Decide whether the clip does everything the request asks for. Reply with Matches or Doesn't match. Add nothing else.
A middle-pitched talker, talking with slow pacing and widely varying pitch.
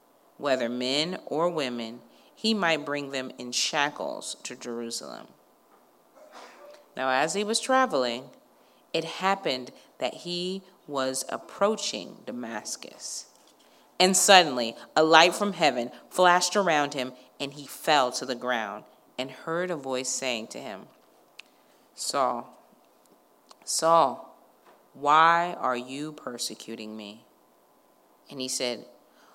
Matches